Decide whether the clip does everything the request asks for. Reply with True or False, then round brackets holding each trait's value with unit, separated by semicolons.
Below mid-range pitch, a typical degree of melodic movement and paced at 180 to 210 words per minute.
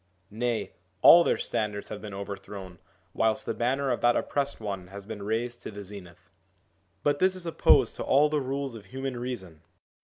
True (115 Hz; 5.0 semitones; 185 wpm)